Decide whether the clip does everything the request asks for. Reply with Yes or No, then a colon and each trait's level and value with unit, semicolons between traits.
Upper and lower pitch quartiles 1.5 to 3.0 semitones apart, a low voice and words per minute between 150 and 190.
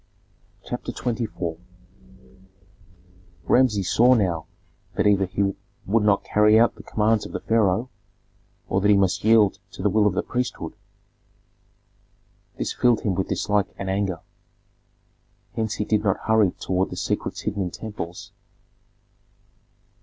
No: narrow, 2.6 semitones; low, 105 Hz; average, 140 wpm